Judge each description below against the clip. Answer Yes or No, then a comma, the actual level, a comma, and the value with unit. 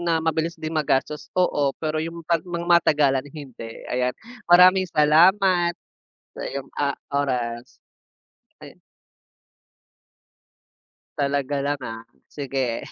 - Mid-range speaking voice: Yes, medium, 150 Hz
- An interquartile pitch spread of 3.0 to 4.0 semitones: Yes, average, 3.7 semitones